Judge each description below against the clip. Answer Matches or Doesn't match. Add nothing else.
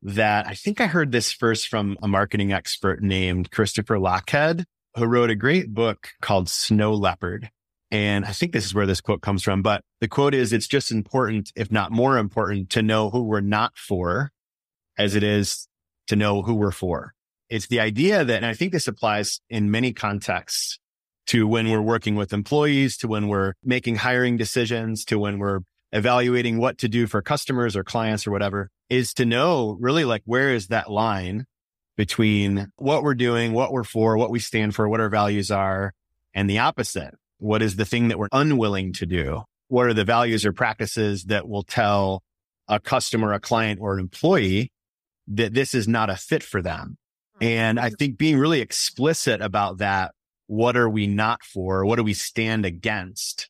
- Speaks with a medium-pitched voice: Doesn't match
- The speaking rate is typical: Matches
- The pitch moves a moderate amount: Matches